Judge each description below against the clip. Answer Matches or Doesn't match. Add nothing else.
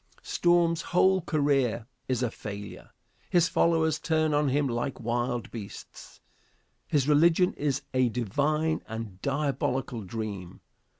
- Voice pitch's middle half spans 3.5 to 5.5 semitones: Matches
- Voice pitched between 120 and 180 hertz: Matches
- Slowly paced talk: Matches